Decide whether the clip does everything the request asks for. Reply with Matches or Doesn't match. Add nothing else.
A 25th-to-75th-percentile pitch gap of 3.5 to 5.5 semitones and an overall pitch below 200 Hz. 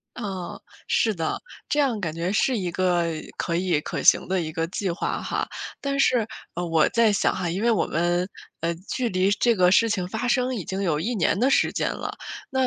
Matches